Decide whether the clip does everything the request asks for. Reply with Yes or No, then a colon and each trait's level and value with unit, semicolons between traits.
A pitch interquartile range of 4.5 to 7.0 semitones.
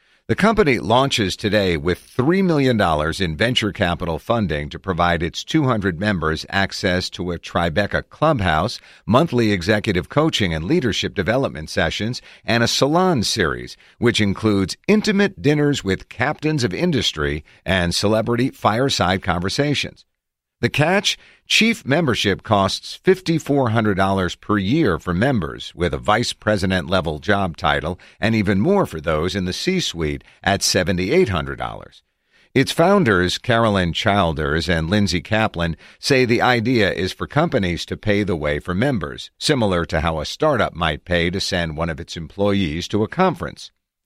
Yes: wide, 5.5 semitones